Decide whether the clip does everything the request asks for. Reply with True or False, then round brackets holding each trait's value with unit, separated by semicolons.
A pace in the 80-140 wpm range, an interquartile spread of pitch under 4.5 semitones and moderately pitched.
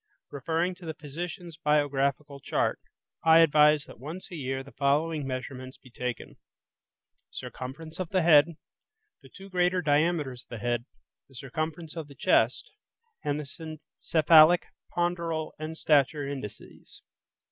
True (135 wpm; 3.1 semitones; 150 Hz)